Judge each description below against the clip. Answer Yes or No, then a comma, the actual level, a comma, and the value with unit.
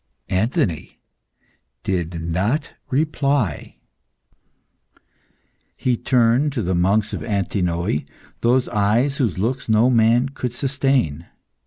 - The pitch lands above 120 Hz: No, low, 115 Hz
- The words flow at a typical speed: No, slow, 100 wpm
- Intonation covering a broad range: Yes, wide, 6.0 semitones